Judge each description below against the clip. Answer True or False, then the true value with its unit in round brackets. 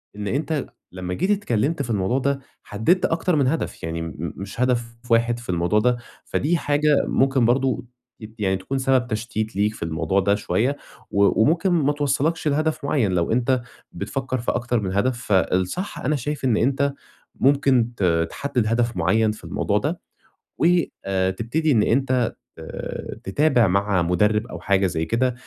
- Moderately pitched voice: False (120 Hz)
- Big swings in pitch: True (5.7 semitones)